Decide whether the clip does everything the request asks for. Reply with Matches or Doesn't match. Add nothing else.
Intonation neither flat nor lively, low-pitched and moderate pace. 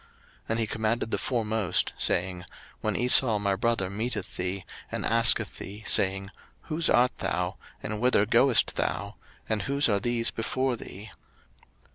Matches